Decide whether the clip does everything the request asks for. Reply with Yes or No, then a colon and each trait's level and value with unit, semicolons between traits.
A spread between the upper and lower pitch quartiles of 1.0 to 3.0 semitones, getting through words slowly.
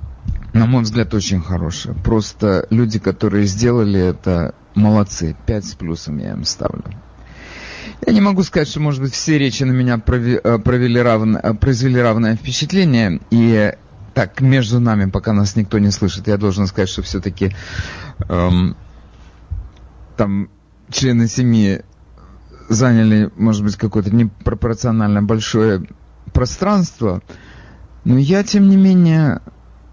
No: average, 3.9 semitones; slow, 130 wpm